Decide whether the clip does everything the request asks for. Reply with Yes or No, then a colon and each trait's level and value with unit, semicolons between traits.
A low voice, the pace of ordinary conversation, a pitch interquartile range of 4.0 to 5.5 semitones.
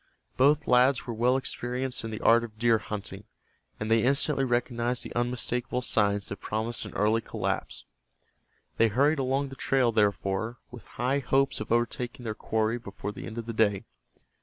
No: low, 120 Hz; average, 175 wpm; narrow, 2.6 semitones